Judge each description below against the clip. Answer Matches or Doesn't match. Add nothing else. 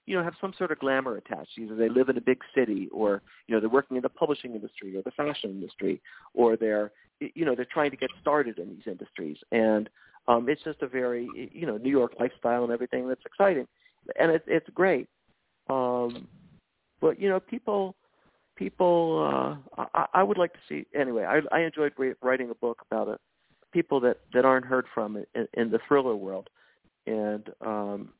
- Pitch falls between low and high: Doesn't match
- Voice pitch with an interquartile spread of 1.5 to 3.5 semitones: Doesn't match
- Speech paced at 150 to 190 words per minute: Doesn't match